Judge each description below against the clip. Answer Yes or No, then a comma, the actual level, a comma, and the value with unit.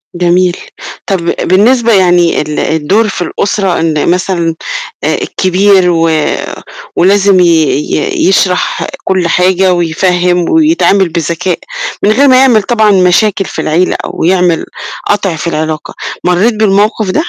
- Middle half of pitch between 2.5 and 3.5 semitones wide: Yes, average, 2.9 semitones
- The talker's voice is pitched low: No, medium, 185 Hz